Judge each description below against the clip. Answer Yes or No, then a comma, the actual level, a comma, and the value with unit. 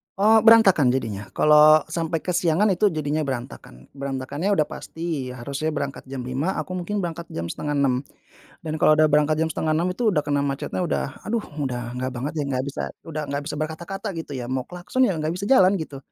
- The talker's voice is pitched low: No, medium, 155 Hz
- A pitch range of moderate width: Yes, average, 4.3 semitones